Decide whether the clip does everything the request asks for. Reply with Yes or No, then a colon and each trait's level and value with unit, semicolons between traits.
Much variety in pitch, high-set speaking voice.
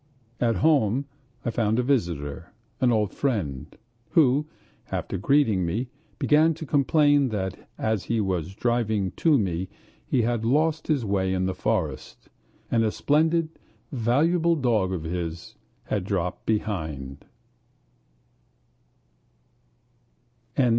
No: wide, 7.1 semitones; low, 110 Hz